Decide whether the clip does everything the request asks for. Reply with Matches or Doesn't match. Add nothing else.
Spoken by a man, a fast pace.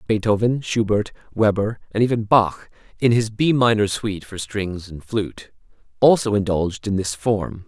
Doesn't match